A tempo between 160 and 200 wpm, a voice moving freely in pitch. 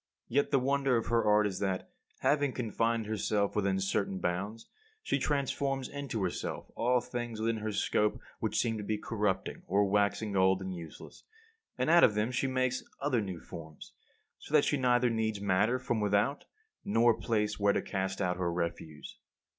No: average, 180 wpm; average, 4.1 semitones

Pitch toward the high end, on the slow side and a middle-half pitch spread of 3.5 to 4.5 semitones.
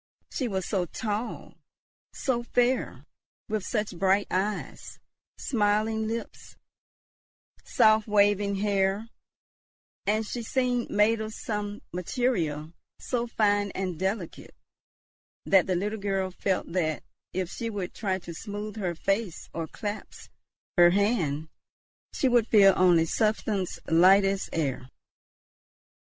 No: high, 205 Hz; slow, 120 wpm; average, 2.9 semitones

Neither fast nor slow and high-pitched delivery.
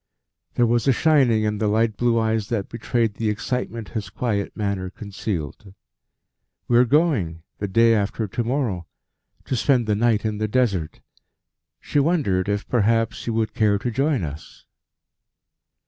No: average, 160 wpm; low, 110 Hz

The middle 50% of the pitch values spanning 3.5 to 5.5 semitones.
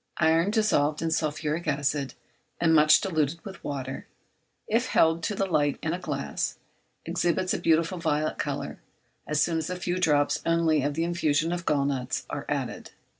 No: average, 2.8 semitones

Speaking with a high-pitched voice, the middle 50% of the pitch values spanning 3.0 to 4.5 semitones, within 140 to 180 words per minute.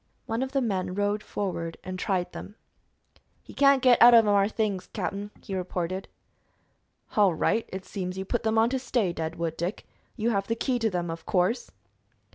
No: high, 200 Hz; average, 3.8 semitones; average, 195 wpm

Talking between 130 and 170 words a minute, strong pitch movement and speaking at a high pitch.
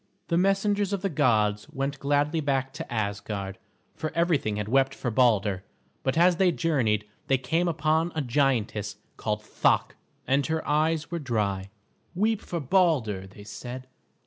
No: average, 155 wpm; wide, 7.4 semitones; low, 135 Hz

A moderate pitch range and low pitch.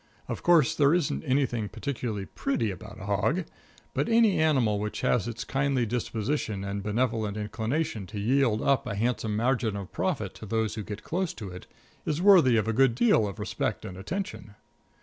Yes: average, 4.9 semitones; low, 115 Hz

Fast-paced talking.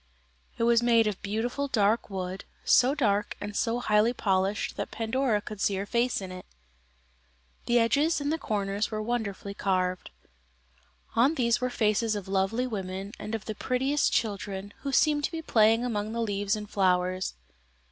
No: average, 170 wpm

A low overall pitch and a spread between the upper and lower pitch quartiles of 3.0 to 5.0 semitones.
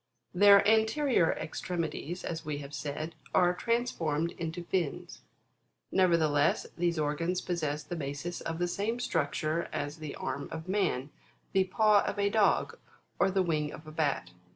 No: medium, 170 Hz; average, 3.8 semitones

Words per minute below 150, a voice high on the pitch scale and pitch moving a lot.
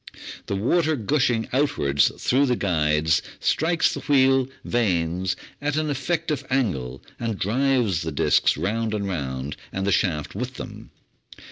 No: average, 140 wpm; low, 110 Hz; wide, 8.4 semitones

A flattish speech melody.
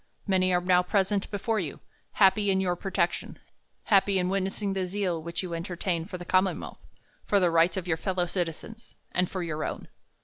Yes: narrow, 1.9 semitones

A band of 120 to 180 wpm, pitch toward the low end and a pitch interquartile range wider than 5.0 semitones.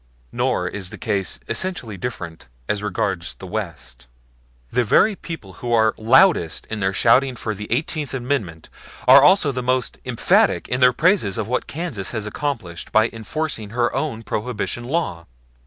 Yes: average, 155 wpm; low, 115 Hz; wide, 5.5 semitones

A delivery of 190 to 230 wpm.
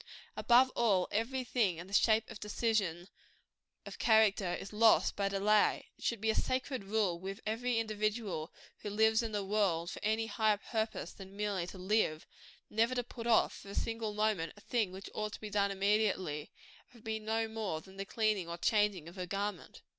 Yes: average, 200 wpm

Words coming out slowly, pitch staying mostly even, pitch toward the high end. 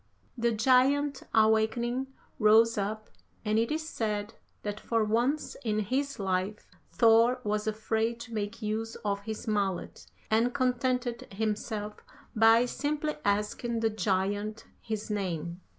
Yes: slow, 130 wpm; narrow, 2.2 semitones; high, 220 Hz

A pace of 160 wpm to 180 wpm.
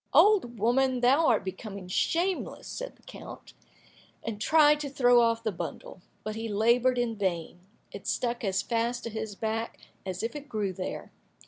Yes: average, 175 wpm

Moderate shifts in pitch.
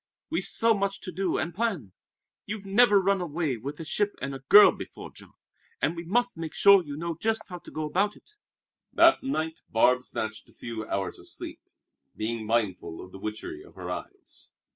No: wide, 8.4 semitones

